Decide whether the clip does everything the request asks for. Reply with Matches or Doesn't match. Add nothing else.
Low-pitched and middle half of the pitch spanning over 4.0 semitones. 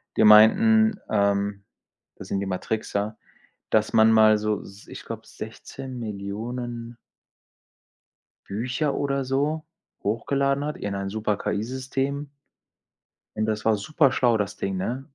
Matches